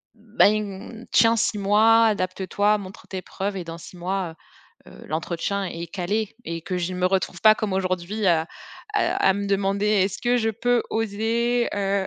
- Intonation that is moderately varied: Yes, average, 3.0 semitones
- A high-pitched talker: Yes, high, 200 Hz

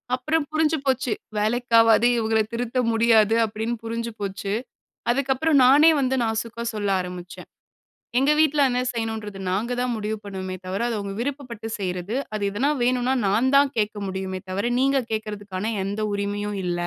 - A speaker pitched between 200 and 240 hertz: Yes, high, 225 Hz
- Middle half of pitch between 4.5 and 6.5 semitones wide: No, average, 3.7 semitones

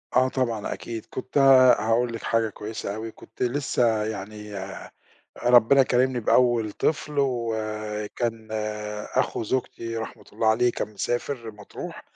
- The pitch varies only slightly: Yes, narrow, 2.3 semitones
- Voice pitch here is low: Yes, low, 115 Hz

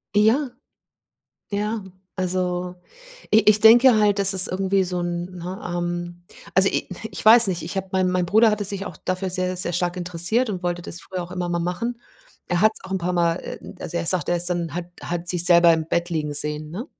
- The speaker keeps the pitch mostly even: Yes, narrow, 2.2 semitones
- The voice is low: No, medium, 180 Hz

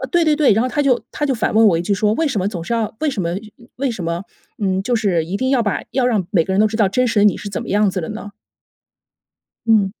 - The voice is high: Yes, high, 215 Hz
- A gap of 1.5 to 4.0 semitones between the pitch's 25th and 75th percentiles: No, average, 4.5 semitones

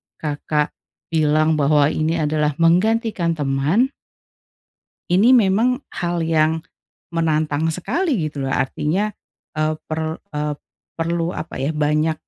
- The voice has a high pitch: No, medium, 160 Hz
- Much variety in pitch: No, narrow, 2.6 semitones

